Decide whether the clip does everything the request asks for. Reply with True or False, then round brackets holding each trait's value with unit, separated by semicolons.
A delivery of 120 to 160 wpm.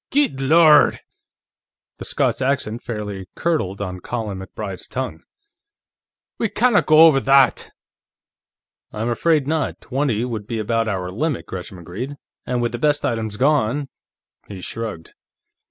True (140 wpm)